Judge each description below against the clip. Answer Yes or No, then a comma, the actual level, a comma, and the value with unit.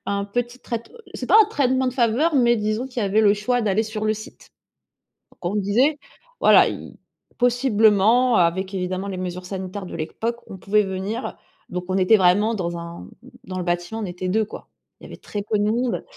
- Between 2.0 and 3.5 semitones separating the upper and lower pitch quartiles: No, average, 4.1 semitones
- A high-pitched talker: Yes, high, 210 Hz